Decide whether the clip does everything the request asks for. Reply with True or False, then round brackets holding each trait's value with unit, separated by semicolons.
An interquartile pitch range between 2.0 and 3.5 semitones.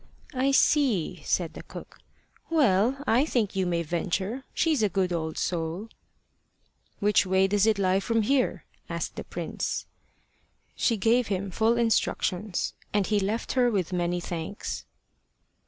False (4.2 semitones)